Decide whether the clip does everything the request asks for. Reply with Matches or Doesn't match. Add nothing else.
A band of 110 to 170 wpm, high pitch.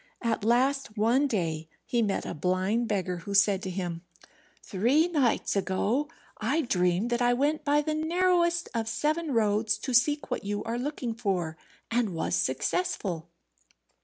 Matches